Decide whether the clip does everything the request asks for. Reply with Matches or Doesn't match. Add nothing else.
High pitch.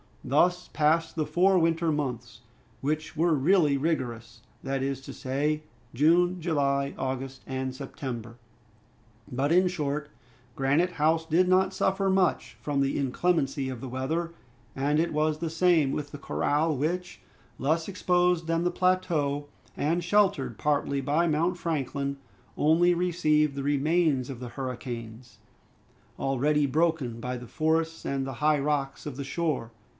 Doesn't match